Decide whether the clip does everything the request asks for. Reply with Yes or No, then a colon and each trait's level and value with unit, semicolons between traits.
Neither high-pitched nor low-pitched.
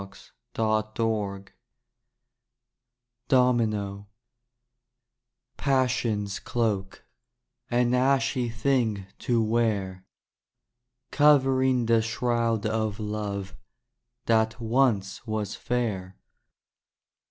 No: low, 115 Hz